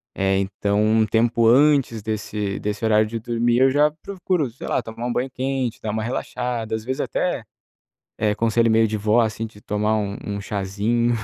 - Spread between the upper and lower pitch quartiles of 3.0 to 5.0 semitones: No, narrow, 2.4 semitones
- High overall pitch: No, low, 110 Hz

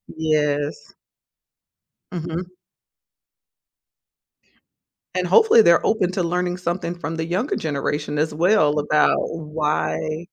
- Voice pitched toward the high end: No, medium, 165 Hz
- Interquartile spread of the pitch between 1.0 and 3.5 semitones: Yes, average, 2.8 semitones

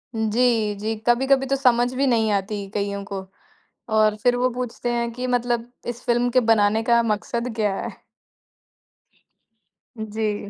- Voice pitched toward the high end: Yes, high, 230 Hz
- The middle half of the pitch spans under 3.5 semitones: Yes, narrow, 2.5 semitones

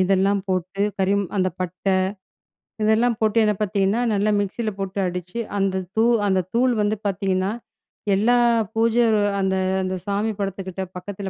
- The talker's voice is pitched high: Yes, high, 200 Hz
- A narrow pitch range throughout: Yes, narrow, 2.2 semitones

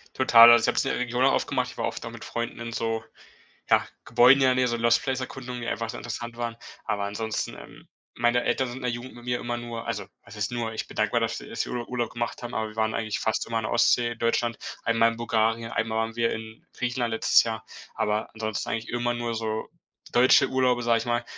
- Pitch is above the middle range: No, low, 120 Hz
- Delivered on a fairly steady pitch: Yes, narrow, 1.3 semitones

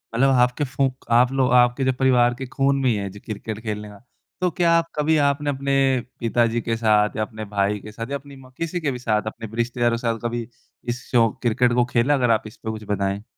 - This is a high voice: No, low, 120 Hz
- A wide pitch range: No, average, 3.5 semitones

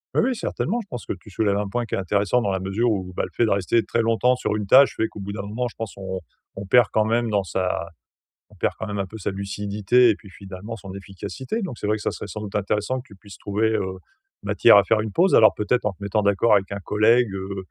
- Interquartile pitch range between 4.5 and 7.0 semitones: No, average, 2.8 semitones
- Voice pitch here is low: Yes, low, 105 Hz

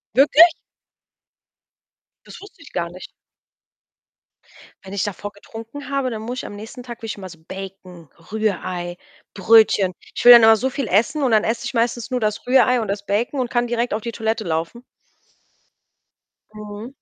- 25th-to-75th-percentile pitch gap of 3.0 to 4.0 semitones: Yes, average, 3.5 semitones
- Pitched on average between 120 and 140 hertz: No, high, 220 Hz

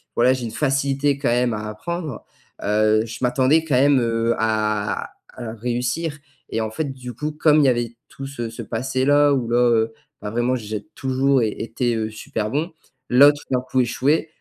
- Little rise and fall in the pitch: No, average, 3.6 semitones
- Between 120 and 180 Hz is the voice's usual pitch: Yes, low, 125 Hz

